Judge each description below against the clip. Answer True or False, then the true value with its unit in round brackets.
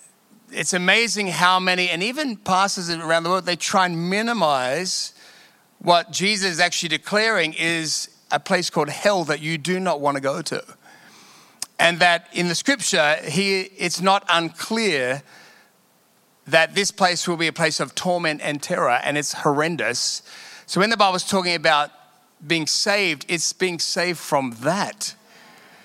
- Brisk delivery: False (160 wpm)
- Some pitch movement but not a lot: True (3.1 semitones)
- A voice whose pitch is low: False (175 Hz)